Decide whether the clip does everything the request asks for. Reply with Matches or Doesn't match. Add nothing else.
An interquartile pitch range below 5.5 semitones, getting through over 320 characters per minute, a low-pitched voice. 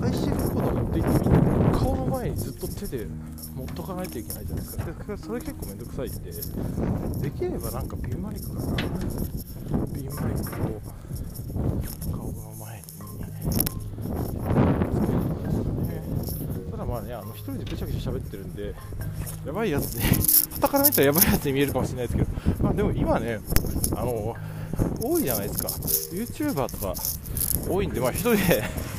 Matches